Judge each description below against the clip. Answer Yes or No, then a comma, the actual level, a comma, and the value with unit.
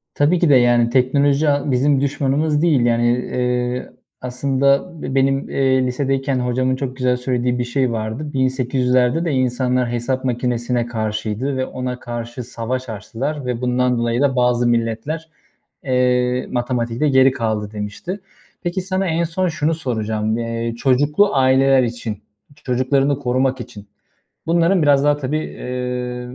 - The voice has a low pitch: Yes, low, 130 Hz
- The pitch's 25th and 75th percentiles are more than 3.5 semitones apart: No, narrow, 2.4 semitones